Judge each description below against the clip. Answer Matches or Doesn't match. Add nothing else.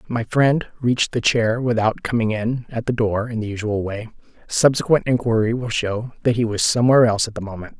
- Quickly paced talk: Matches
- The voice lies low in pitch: Matches